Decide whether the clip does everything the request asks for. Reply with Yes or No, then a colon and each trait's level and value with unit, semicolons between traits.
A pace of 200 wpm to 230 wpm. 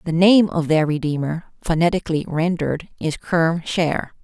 No: average, 140 wpm